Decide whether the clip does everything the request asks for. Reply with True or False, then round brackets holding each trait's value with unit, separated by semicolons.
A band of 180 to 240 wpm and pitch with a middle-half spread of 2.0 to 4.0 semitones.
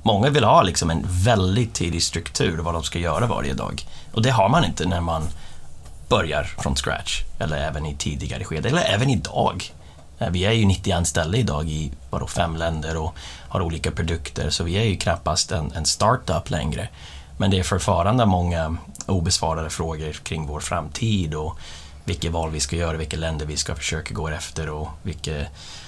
True (185 wpm; 3.0 semitones)